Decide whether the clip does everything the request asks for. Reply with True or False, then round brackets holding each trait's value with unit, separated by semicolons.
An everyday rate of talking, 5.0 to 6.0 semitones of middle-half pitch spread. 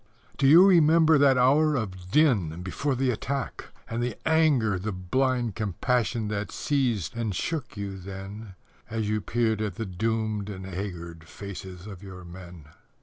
True (155 wpm; 5.4 semitones)